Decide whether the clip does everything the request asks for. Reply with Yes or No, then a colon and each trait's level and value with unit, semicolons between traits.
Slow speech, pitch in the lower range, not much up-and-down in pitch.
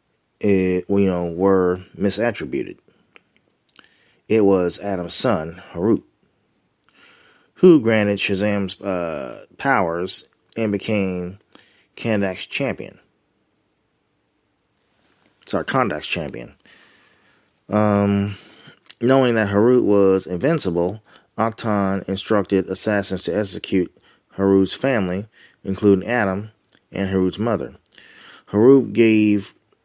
Yes: slow, 85 wpm; low, 100 Hz; narrow, 2.1 semitones